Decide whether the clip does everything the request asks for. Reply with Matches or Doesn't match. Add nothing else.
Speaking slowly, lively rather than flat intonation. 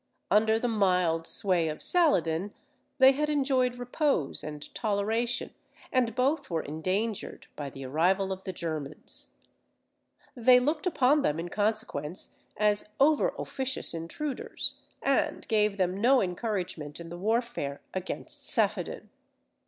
Matches